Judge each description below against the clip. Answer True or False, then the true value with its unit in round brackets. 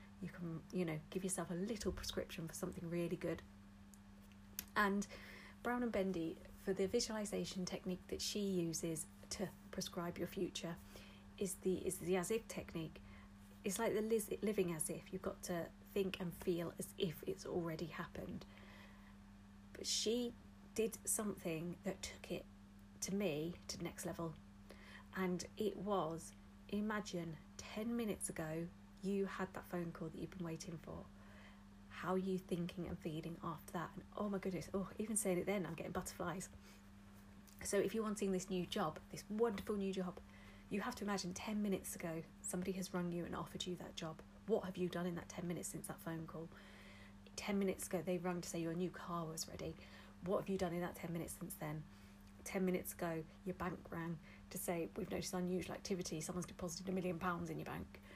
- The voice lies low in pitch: False (175 Hz)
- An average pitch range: True (3.3 semitones)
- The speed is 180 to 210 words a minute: True (190 wpm)